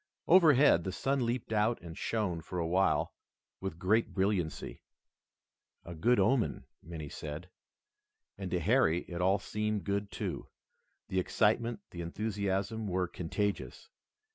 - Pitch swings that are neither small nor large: Yes, average, 3.9 semitones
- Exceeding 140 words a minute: No, slow, 135 wpm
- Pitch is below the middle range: Yes, low, 100 Hz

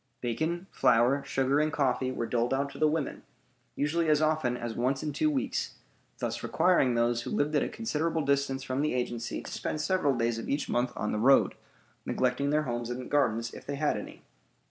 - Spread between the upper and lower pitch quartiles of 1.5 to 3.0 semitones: No, average, 3.8 semitones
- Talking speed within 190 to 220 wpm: Yes, fast, 205 wpm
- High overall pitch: No, low, 135 Hz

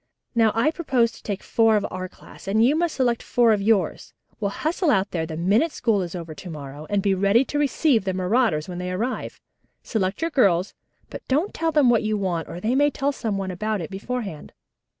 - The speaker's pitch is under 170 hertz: No, high, 215 Hz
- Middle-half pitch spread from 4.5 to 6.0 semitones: Yes, wide, 5.4 semitones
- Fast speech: Yes, fast, 225 wpm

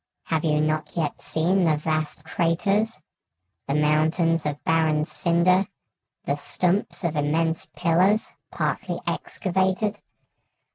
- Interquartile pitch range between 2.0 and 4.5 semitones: Yes, average, 3.0 semitones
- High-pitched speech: No, medium, 165 Hz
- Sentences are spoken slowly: Yes, slow, 110 wpm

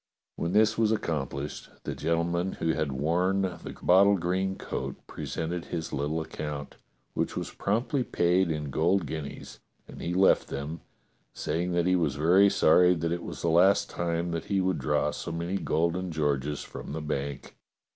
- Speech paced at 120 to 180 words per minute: Yes, average, 170 wpm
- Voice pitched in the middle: No, very low, 85 Hz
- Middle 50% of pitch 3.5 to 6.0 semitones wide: No, average, 3.1 semitones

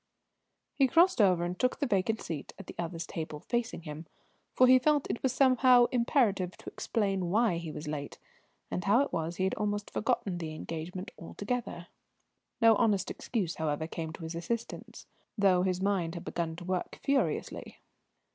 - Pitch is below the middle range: No, high, 190 Hz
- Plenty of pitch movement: Yes, wide, 6.0 semitones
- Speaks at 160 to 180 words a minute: Yes, average, 175 wpm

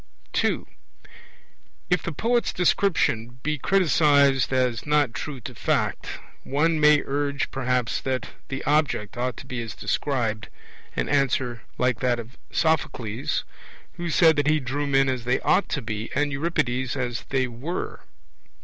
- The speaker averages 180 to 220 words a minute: No, average, 150 wpm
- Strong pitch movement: No, average, 3.5 semitones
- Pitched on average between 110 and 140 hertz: Yes, low, 135 Hz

